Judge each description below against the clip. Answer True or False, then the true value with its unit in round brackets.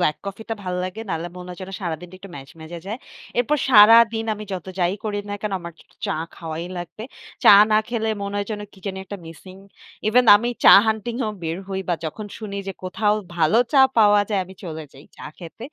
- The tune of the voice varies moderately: True (3.7 semitones)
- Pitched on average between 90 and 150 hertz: False (195 Hz)